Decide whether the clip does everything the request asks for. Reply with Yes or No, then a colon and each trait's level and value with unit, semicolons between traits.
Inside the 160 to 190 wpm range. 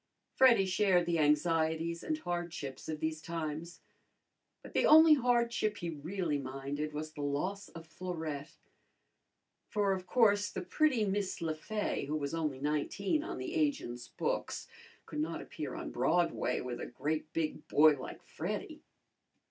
No: average, 150 wpm